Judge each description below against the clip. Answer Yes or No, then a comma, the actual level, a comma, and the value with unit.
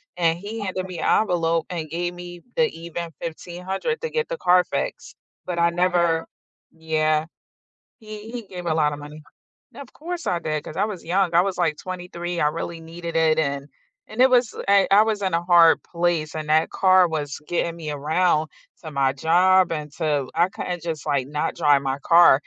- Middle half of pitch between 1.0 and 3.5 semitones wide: Yes, average, 2.8 semitones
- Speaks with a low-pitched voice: No, medium, 170 Hz